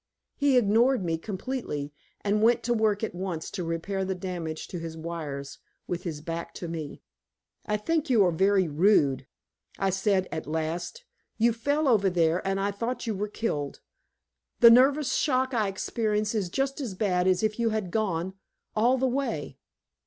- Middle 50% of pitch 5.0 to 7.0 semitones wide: Yes, wide, 5.4 semitones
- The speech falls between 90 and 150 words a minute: No, average, 175 wpm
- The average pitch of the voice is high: Yes, high, 195 Hz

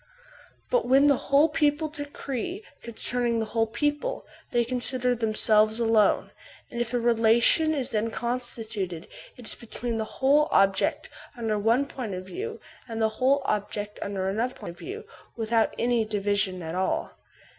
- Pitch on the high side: Yes, high, 235 Hz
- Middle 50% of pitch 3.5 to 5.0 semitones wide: Yes, average, 4.0 semitones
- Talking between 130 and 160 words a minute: Yes, average, 155 wpm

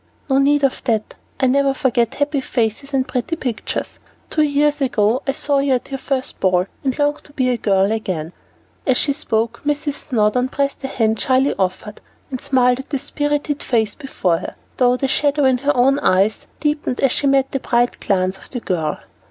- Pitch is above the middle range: Yes, very high, 260 Hz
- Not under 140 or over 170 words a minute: No, average, 200 wpm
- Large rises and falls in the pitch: No, average, 4.0 semitones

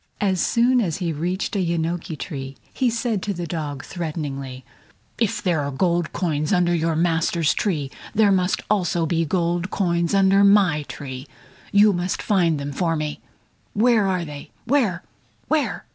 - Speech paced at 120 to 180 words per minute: Yes, average, 160 wpm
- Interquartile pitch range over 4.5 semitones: No, average, 3.9 semitones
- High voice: No, medium, 175 Hz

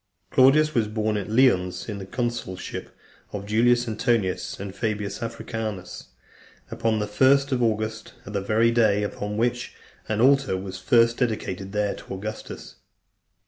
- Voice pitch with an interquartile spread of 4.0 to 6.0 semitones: No, average, 2.7 semitones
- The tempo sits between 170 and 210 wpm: No, average, 145 wpm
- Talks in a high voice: No, low, 110 Hz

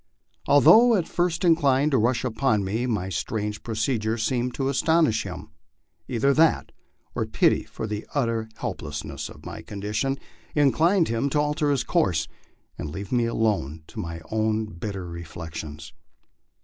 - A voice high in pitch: No, low, 115 Hz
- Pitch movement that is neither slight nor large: No, wide, 5.9 semitones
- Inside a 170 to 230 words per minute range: No, average, 150 wpm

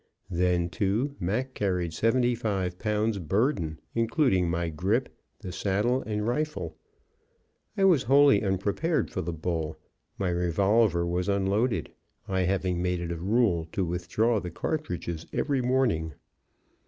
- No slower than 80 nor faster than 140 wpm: Yes, slow, 135 wpm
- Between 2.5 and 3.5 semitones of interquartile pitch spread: No, average, 5.1 semitones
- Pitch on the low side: Yes, very low, 95 Hz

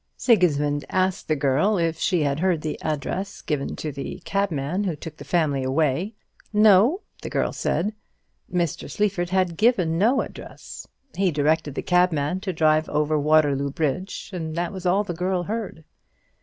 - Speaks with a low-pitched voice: No, medium, 170 Hz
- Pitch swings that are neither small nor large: Yes, average, 4.0 semitones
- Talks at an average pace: Yes, average, 165 wpm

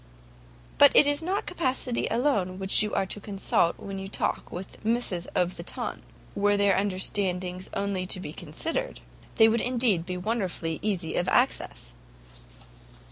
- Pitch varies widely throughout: No, average, 4.1 semitones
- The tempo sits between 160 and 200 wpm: No, average, 150 wpm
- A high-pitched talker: Yes, high, 195 Hz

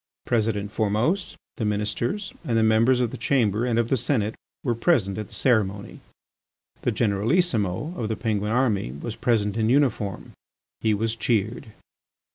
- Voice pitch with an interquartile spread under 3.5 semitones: Yes, average, 2.9 semitones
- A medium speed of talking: Yes, average, 155 wpm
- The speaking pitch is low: Yes, low, 110 Hz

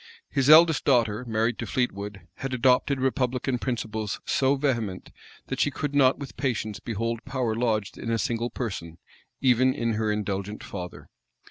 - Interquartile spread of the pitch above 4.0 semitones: No, average, 3.5 semitones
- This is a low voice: Yes, low, 120 Hz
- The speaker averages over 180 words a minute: No, average, 155 wpm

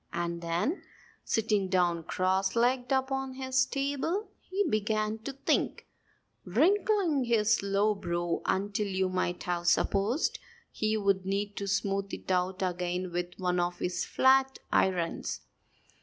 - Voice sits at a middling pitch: No, high, 200 Hz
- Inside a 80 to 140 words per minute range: Yes, slow, 135 wpm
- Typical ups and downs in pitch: No, wide, 6.2 semitones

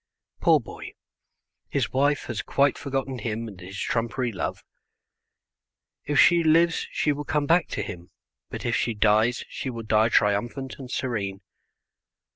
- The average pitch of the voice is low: Yes, low, 120 Hz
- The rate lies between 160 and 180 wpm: No, average, 150 wpm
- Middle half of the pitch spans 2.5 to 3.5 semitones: No, average, 4.7 semitones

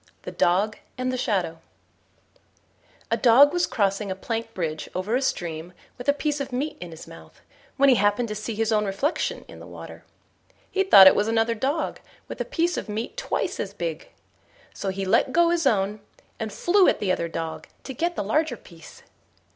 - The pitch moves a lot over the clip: Yes, wide, 6.5 semitones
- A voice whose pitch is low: No, high, 225 Hz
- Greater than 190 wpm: Yes, average, 200 wpm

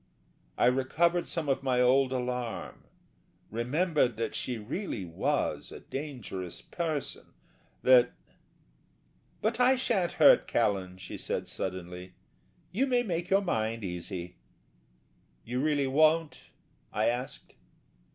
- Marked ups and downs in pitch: Yes, wide, 7.0 semitones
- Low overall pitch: Yes, low, 130 Hz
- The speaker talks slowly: Yes, slow, 115 wpm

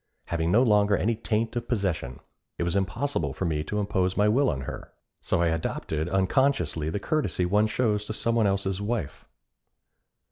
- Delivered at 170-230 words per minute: Yes, average, 180 wpm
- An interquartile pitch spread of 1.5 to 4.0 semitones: No, average, 4.5 semitones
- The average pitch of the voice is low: Yes, low, 100 Hz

